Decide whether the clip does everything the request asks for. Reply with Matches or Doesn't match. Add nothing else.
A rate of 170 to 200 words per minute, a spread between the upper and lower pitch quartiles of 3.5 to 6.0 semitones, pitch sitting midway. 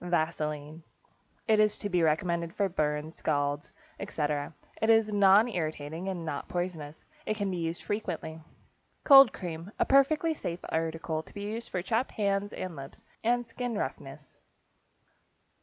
Doesn't match